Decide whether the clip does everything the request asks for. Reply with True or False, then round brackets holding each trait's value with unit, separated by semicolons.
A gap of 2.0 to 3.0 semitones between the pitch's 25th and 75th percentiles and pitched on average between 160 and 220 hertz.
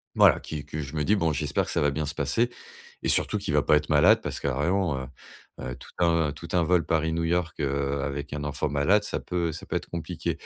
False (2.7 semitones; 75 Hz)